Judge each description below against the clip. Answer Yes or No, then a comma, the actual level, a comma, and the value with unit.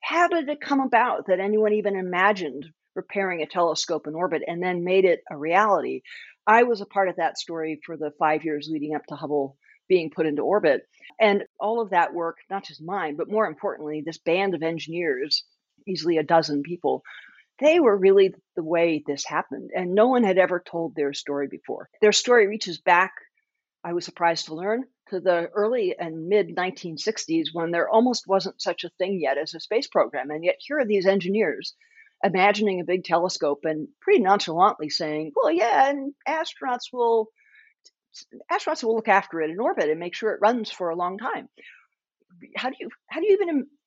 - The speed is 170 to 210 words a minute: Yes, average, 195 wpm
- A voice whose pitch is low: No, medium, 185 Hz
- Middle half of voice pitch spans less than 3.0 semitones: No, wide, 5.6 semitones